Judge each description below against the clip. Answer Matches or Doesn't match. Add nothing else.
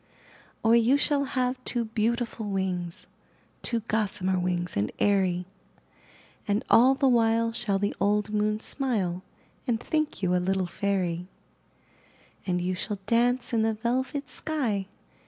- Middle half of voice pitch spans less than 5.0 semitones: Matches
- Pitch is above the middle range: Matches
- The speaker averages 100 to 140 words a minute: Doesn't match